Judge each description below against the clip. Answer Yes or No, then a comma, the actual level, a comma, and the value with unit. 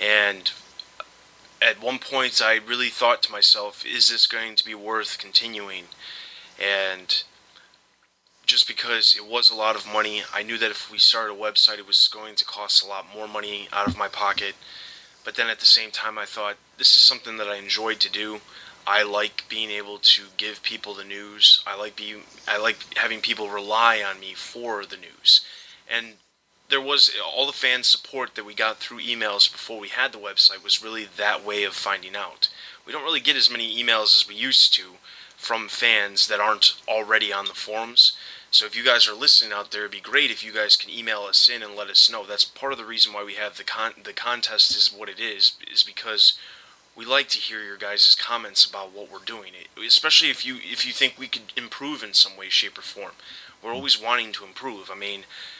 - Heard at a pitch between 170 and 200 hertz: No, low, 105 Hz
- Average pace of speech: No, fast, 215 wpm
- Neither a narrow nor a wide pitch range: No, narrow, 1.8 semitones